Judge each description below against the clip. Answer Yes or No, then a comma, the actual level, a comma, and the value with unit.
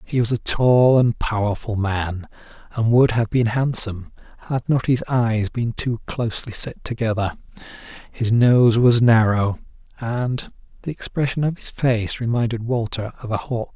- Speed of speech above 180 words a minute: No, average, 155 wpm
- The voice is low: Yes, low, 115 Hz